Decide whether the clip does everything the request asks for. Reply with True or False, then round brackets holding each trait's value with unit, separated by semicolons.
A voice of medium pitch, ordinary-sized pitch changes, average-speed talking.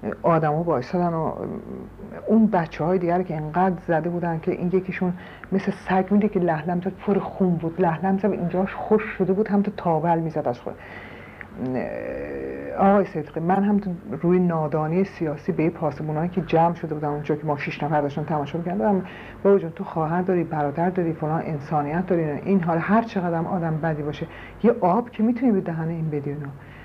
False (175 Hz; 3.3 semitones; 185 wpm)